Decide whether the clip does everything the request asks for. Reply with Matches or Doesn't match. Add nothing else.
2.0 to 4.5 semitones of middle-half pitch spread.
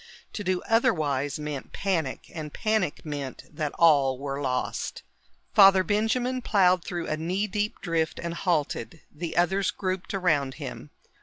Doesn't match